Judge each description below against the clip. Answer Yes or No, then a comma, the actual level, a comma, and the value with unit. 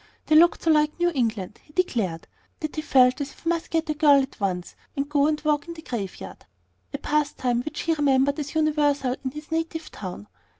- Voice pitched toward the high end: Yes, very high, 295 Hz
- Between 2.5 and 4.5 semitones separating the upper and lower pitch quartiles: Yes, average, 3.5 semitones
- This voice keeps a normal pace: No, fast, 215 wpm